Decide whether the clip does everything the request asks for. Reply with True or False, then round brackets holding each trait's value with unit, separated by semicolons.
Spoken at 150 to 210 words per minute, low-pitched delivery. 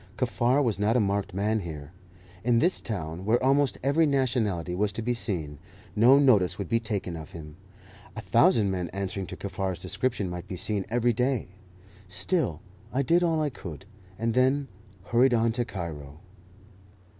True (170 wpm; 110 Hz)